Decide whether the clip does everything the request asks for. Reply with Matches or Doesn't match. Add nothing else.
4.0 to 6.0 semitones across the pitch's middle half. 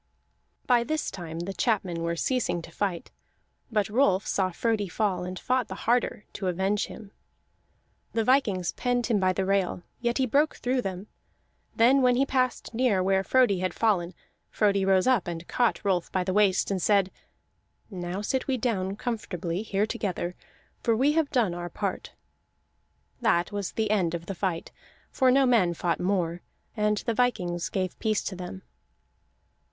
Matches